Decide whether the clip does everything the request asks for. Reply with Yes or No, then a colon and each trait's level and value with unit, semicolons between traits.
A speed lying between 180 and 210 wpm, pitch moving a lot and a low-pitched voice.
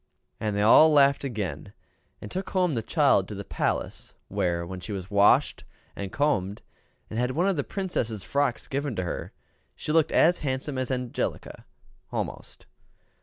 No: average, 170 wpm; wide, 6.4 semitones; low, 125 Hz